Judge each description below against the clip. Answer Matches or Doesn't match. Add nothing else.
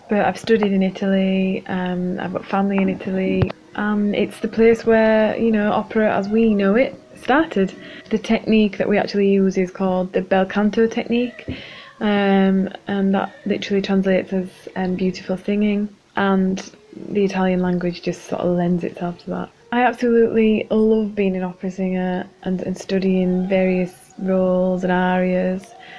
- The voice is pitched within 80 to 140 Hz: Doesn't match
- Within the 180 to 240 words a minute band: Doesn't match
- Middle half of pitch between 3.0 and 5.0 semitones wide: Doesn't match